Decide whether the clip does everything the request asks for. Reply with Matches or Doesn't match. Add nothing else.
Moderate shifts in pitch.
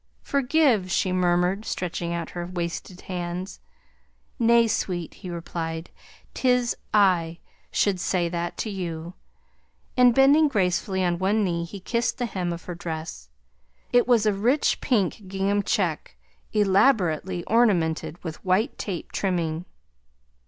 Matches